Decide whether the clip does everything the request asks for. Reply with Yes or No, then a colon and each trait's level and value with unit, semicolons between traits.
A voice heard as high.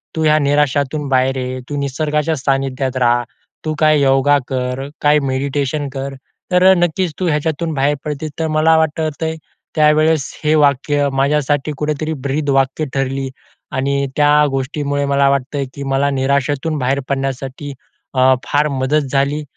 No: medium, 140 Hz